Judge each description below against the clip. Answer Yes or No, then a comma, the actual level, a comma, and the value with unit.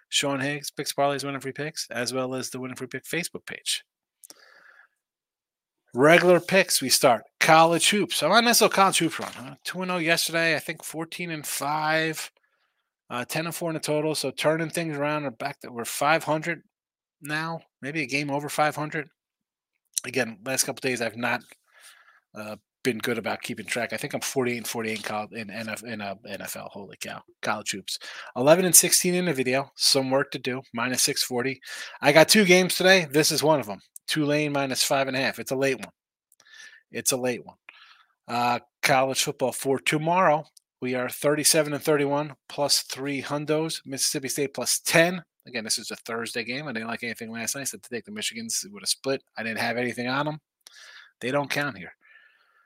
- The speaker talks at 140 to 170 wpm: No, average, 190 wpm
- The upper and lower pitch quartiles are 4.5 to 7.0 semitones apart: No, average, 4.1 semitones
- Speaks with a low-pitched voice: No, medium, 145 Hz